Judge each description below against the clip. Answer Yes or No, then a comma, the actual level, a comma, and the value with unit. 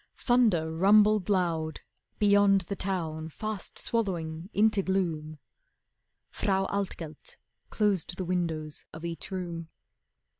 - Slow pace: Yes, slow, 105 wpm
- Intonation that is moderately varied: Yes, average, 3.9 semitones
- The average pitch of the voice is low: No, medium, 185 Hz